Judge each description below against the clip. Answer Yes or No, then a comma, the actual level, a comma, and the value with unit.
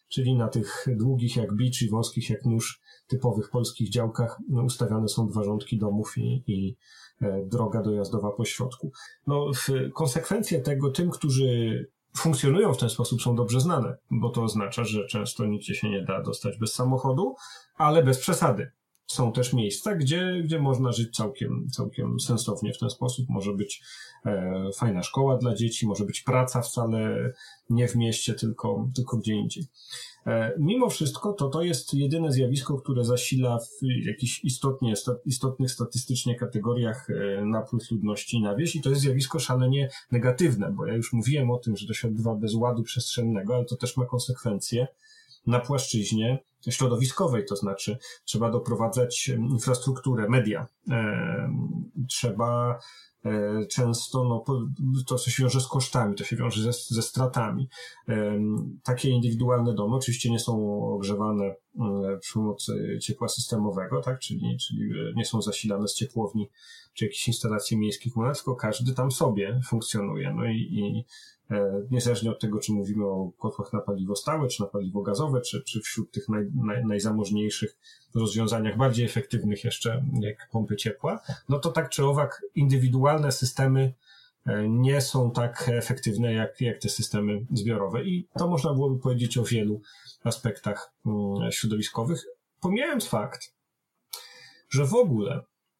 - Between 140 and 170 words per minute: Yes, average, 155 wpm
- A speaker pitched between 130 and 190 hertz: No, low, 120 Hz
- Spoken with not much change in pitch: No, average, 3.3 semitones